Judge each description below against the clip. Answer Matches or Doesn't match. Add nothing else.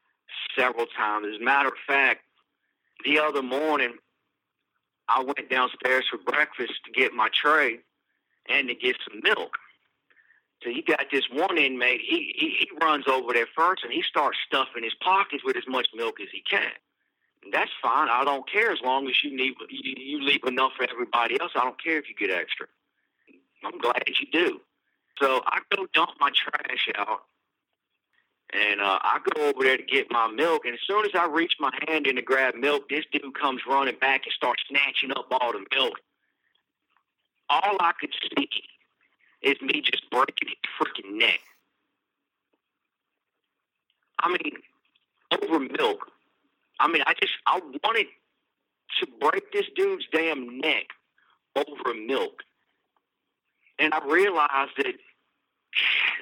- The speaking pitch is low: Doesn't match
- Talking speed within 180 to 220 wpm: Doesn't match